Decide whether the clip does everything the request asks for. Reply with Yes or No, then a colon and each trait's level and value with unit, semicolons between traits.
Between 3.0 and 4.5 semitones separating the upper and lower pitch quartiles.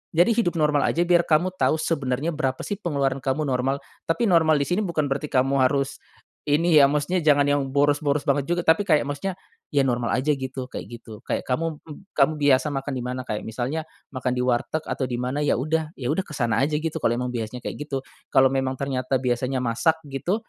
Yes: average, 3.4 semitones